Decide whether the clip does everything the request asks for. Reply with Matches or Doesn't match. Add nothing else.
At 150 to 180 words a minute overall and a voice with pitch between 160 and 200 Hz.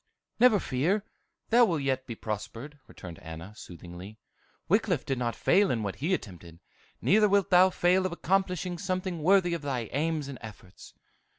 Doesn't match